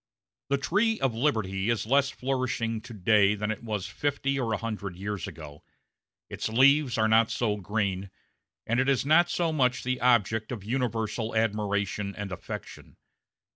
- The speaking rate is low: No, average, 165 wpm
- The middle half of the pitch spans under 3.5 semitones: No, average, 4.2 semitones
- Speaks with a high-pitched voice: No, low, 115 Hz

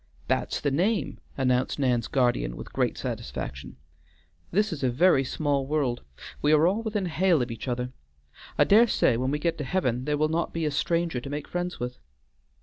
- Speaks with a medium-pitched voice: Yes, medium, 145 Hz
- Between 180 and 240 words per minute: Yes, average, 195 wpm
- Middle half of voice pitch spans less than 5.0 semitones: No, average, 5.3 semitones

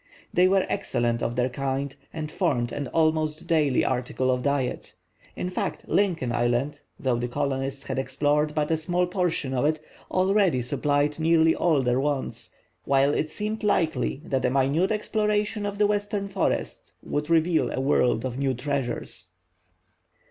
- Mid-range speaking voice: Yes, medium, 145 Hz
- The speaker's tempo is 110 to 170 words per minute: Yes, average, 160 wpm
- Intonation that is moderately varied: Yes, average, 5.0 semitones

